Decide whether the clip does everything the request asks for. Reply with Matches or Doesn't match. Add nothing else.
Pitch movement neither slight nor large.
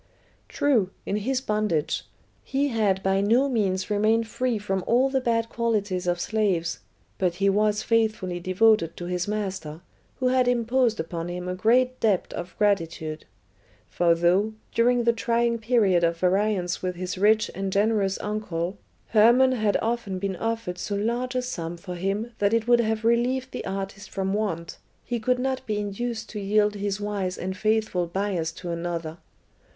Matches